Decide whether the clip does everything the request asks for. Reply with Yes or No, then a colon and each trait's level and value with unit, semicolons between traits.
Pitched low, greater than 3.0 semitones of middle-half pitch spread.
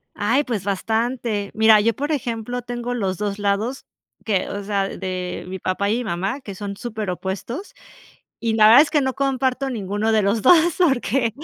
No: high, 220 Hz; average, 3.7 semitones